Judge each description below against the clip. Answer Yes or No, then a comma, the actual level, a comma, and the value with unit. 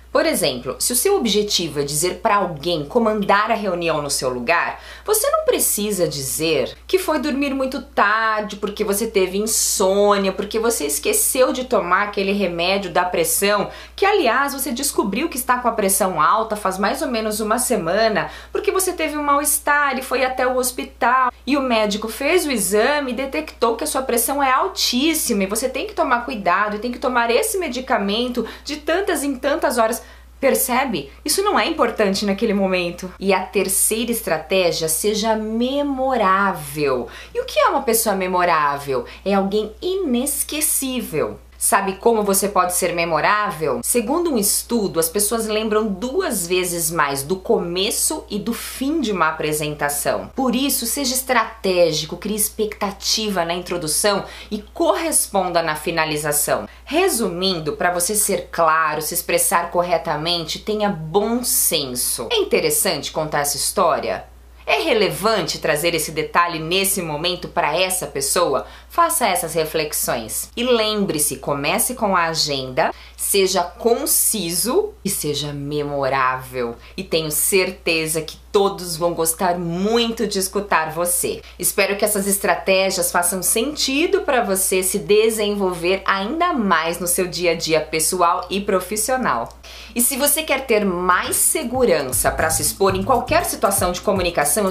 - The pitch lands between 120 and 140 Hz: No, high, 205 Hz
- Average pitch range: No, wide, 6.2 semitones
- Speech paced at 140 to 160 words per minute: Yes, average, 150 wpm